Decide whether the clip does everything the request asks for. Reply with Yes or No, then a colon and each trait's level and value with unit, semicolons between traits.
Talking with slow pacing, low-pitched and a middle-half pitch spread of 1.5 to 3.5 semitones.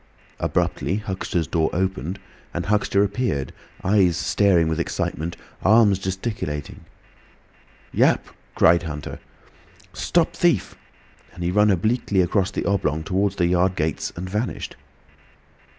Yes: slow, 120 wpm; very low, 95 Hz; average, 3.0 semitones